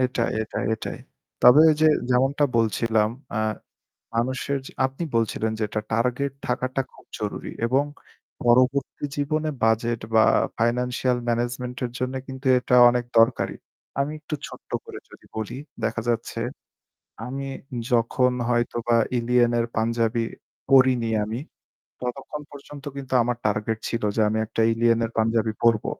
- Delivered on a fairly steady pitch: Yes, narrow, 2.2 semitones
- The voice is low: Yes, low, 120 Hz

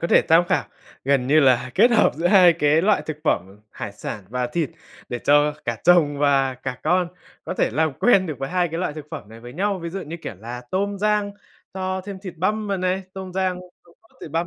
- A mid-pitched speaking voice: Yes, medium, 165 Hz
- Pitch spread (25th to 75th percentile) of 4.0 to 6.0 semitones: Yes, wide, 5.5 semitones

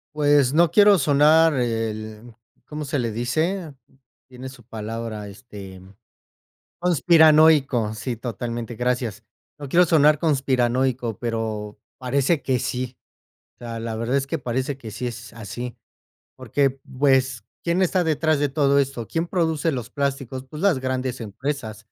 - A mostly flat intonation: No, average, 4.2 semitones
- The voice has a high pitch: No, low, 130 Hz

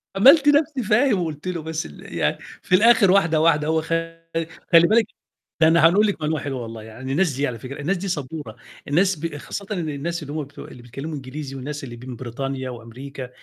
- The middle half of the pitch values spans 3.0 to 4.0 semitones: No, average, 5.3 semitones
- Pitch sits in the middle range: Yes, medium, 155 Hz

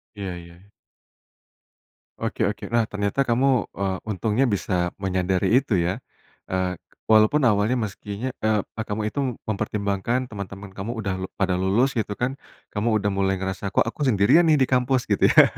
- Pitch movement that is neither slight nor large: Yes, average, 3.6 semitones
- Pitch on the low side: Yes, low, 105 Hz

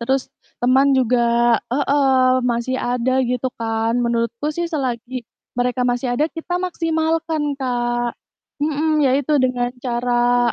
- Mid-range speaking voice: No, very high, 255 Hz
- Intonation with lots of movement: No, average, 3.2 semitones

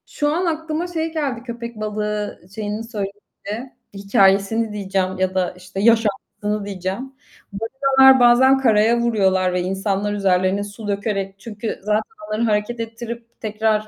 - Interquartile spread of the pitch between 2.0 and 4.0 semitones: Yes, average, 3.0 semitones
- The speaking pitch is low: No, high, 215 Hz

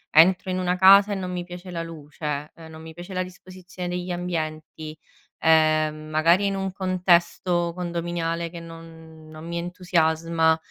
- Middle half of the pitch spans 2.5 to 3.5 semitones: No, narrow, 2.1 semitones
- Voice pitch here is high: No, medium, 170 Hz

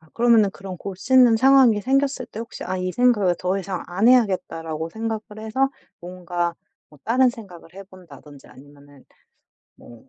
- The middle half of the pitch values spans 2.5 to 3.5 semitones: No, average, 5.3 semitones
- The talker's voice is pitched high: Yes, high, 195 Hz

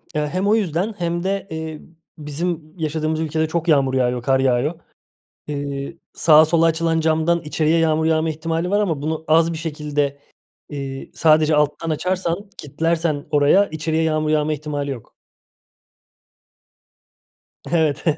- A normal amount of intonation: No, narrow, 1.9 semitones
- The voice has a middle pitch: Yes, medium, 155 Hz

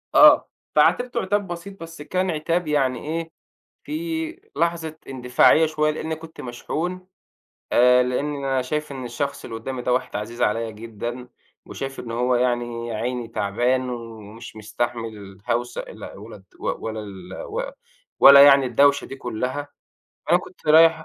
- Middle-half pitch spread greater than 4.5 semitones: Yes, average, 5.1 semitones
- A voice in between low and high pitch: No, low, 130 Hz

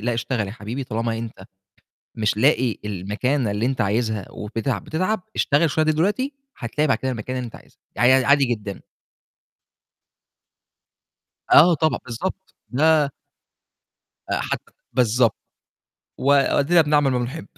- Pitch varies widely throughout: No, average, 4.7 semitones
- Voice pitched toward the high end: No, low, 125 Hz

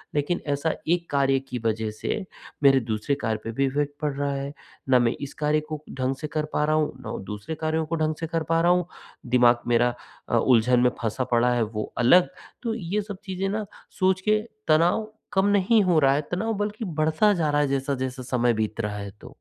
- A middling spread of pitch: No, wide, 5.8 semitones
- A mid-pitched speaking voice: Yes, medium, 145 Hz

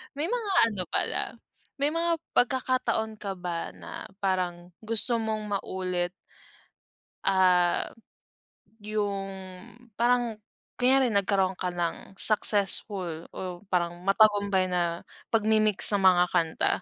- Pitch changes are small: No, average, 3.5 semitones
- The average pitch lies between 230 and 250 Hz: No, high, 200 Hz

